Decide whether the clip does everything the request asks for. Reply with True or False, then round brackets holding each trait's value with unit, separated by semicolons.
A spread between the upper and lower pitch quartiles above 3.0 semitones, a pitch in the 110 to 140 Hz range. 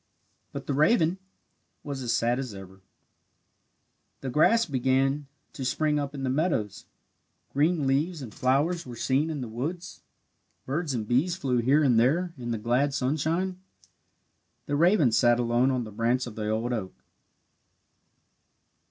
True (4.3 semitones; 135 Hz)